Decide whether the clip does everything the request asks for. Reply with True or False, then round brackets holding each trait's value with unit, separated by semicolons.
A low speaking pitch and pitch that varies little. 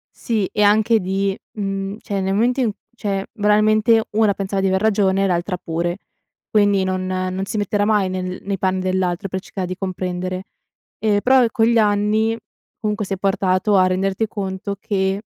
False (195 Hz; 2.0 semitones)